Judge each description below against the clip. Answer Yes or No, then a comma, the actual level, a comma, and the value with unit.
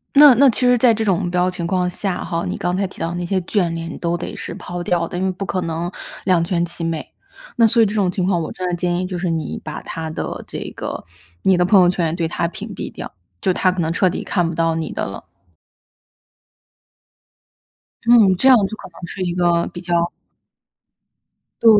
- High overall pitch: No, medium, 180 Hz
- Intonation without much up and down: Yes, narrow, 2.0 semitones